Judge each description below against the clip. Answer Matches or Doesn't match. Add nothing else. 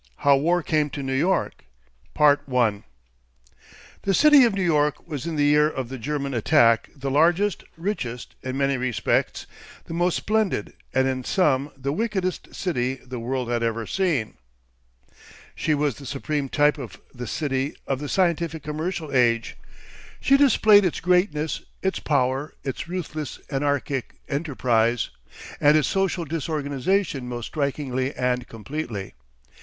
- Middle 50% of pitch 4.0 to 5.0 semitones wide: Matches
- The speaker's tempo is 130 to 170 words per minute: Matches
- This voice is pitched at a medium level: Matches